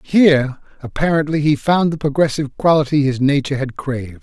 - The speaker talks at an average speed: Yes, average, 155 wpm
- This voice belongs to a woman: No, male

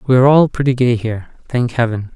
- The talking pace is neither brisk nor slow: No, fast, 220 wpm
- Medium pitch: No, low, 120 Hz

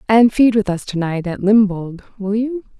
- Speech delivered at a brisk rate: Yes, fast, 215 wpm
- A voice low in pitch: No, high, 210 Hz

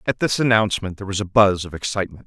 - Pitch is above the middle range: No, low, 100 Hz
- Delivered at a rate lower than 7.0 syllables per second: No, 7.4 syllables/s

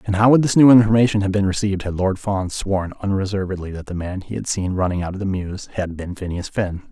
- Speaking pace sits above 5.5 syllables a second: Yes, 6.1 syllables/s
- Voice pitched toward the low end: Yes, very low, 95 Hz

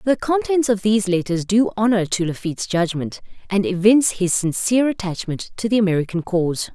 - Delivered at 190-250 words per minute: No, average, 170 wpm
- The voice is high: Yes, high, 200 Hz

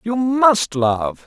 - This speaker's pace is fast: No, average, 140 wpm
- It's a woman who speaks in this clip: No, male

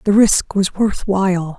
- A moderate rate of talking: Yes, average, 190 wpm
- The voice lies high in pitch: Yes, high, 195 Hz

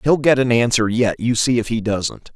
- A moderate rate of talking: No, fast, 255 wpm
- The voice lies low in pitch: Yes, low, 115 Hz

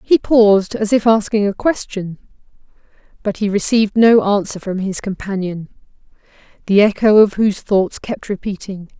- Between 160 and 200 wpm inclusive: No, average, 145 wpm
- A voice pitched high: Yes, high, 205 Hz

